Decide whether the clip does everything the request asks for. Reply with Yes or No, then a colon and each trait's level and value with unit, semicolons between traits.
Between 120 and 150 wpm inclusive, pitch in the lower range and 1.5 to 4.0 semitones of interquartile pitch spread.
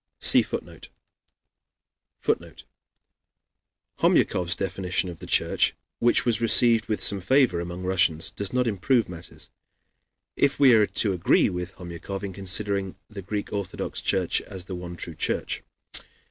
Yes: average, 140 wpm; very low, 95 Hz; average, 3.2 semitones